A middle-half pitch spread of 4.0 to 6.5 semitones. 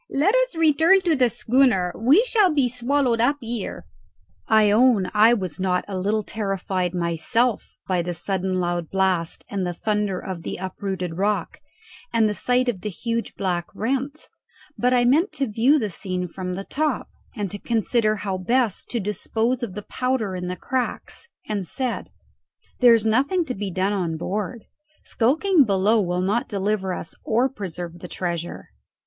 Yes: average, 5.1 semitones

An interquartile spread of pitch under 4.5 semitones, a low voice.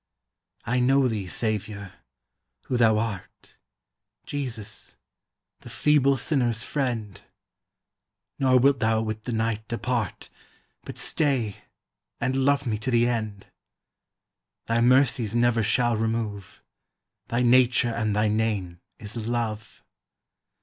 Yes: narrow, 2.6 semitones; low, 115 Hz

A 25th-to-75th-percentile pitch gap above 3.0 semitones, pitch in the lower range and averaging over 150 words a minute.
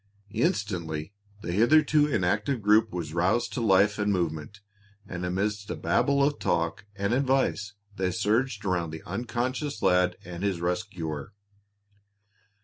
No: average, 4.9 semitones; low, 100 Hz; slow, 135 wpm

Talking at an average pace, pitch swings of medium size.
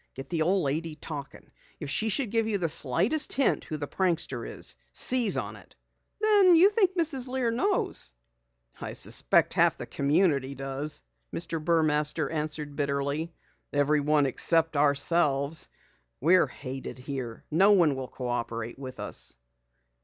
No: average, 145 wpm; wide, 5.8 semitones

